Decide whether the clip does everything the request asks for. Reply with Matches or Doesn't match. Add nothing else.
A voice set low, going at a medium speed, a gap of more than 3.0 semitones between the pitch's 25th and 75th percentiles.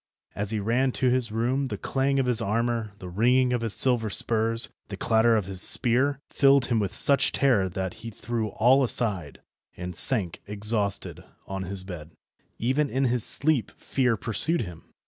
Matches